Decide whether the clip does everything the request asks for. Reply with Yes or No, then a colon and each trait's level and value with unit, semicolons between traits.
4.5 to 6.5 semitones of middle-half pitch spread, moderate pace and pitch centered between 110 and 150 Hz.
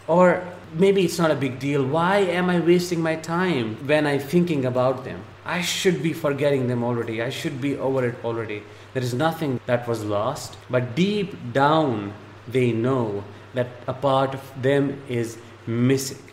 Yes: average, 5.1 semitones; average, 175 wpm; low, 135 Hz